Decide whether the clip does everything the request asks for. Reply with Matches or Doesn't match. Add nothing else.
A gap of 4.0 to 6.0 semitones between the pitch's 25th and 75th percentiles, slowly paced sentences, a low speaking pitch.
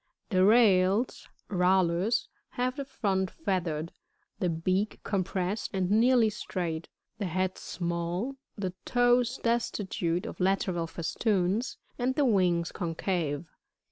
Doesn't match